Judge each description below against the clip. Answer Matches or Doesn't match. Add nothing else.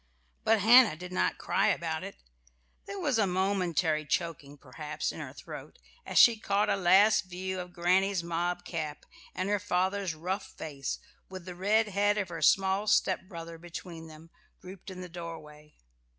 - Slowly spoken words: Doesn't match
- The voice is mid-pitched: Matches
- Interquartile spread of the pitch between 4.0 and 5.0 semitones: Doesn't match